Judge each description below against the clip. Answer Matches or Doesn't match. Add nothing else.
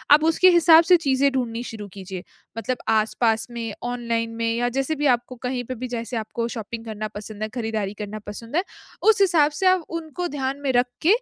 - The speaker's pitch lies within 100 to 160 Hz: Doesn't match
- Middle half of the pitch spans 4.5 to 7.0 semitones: Matches